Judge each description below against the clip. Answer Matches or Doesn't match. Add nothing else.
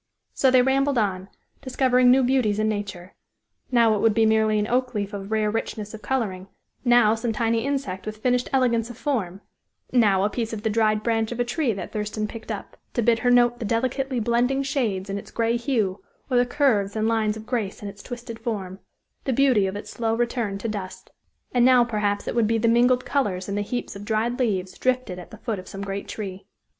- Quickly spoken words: Matches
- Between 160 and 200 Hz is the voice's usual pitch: Doesn't match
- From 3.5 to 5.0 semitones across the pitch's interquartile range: Doesn't match